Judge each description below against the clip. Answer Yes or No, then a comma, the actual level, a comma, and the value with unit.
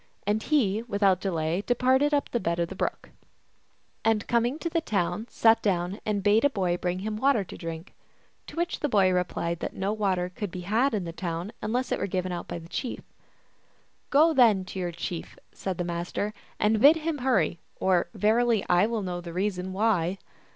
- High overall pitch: Yes, high, 200 Hz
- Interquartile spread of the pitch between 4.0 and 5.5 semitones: Yes, average, 4.6 semitones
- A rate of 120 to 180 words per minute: No, fast, 205 wpm